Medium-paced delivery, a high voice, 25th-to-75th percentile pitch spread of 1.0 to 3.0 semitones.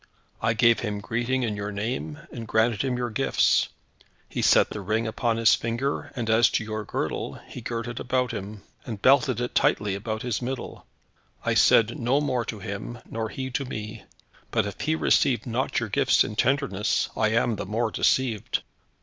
No: average, 190 wpm; low, 115 Hz; narrow, 2.5 semitones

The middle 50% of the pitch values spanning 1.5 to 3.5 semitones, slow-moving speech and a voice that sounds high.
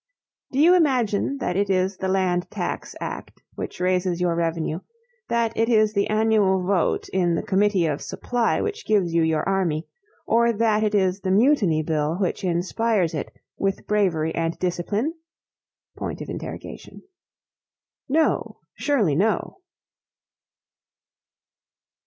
No: average, 4.2 semitones; slow, 130 wpm; high, 195 Hz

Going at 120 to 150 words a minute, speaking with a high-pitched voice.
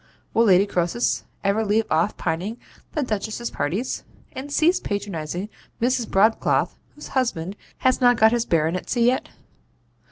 Yes: slow, 135 wpm; high, 220 Hz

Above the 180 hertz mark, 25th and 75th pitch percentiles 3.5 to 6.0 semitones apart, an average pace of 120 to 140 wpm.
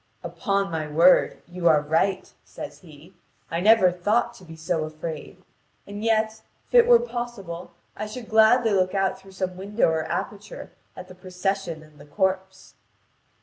No: high, 190 Hz; average, 4.0 semitones; average, 165 wpm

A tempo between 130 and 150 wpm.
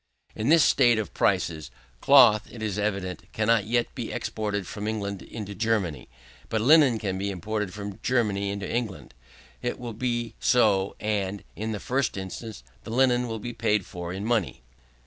No: average, 170 wpm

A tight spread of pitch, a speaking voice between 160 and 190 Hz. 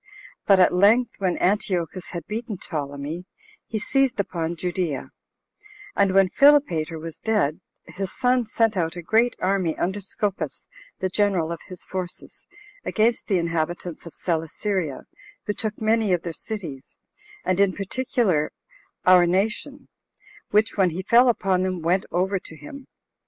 No: average, 3.9 semitones; medium, 185 Hz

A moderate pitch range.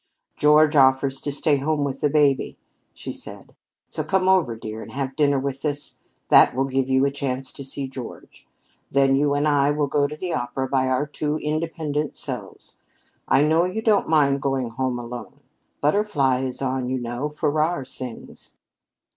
No: narrow, 2.3 semitones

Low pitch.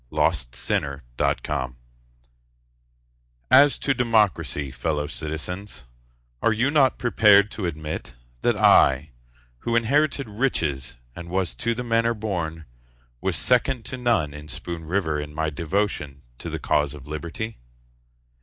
Yes: very low, 90 Hz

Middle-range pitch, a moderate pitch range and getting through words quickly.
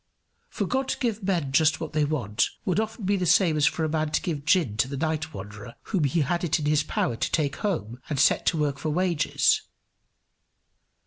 Yes: medium, 155 Hz; average, 4.0 semitones; fast, 220 wpm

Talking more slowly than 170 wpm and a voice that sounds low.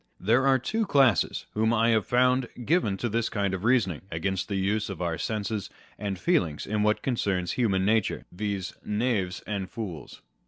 No: average, 175 wpm; low, 105 Hz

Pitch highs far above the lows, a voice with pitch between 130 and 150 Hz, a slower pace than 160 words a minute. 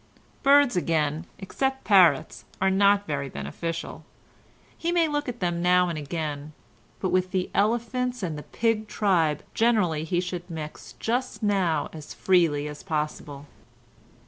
No: wide, 5.8 semitones; medium, 180 Hz; average, 145 wpm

